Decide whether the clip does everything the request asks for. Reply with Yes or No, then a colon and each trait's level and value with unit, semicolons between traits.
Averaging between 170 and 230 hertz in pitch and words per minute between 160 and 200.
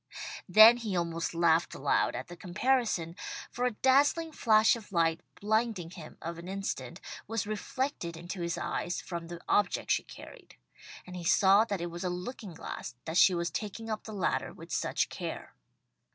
Yes: medium, 185 Hz; average, 180 wpm